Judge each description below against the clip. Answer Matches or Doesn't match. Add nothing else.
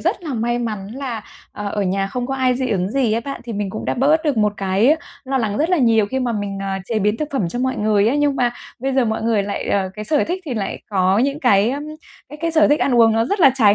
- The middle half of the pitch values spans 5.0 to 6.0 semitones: Doesn't match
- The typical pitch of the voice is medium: Doesn't match